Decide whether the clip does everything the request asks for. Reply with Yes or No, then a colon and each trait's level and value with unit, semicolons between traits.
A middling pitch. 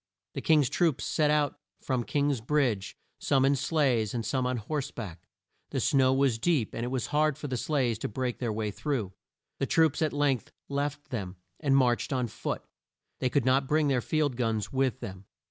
No: low, 130 Hz